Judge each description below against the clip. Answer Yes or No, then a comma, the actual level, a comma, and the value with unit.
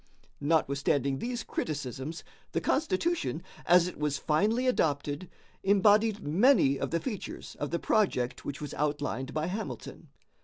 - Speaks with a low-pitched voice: No, medium, 160 Hz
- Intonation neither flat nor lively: No, wide, 6.5 semitones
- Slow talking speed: Yes, slow, 130 wpm